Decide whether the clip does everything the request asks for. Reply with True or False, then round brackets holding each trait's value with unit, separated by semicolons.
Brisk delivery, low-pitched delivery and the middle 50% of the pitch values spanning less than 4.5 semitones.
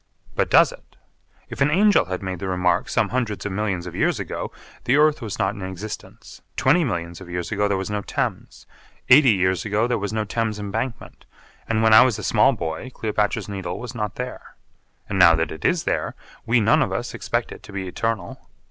True (215 wpm; 105 Hz; 3.6 semitones)